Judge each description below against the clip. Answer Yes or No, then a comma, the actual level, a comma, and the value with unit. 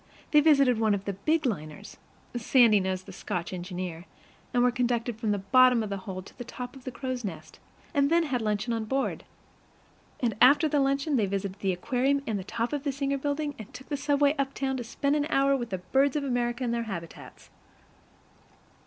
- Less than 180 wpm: No, fast, 205 wpm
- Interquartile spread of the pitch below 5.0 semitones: No, average, 5.3 semitones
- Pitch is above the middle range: Yes, high, 245 Hz